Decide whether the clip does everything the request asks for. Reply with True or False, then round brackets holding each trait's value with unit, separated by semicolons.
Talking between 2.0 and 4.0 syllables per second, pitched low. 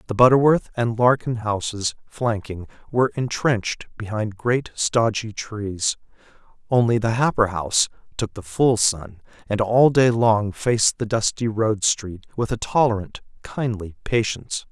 False (4.4 syllables/s; 110 Hz)